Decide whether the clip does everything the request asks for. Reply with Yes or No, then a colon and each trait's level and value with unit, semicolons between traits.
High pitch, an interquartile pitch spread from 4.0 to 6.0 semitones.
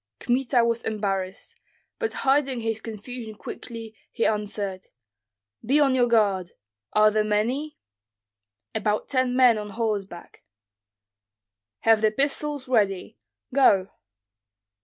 No: high, 225 Hz; average, 3.4 semitones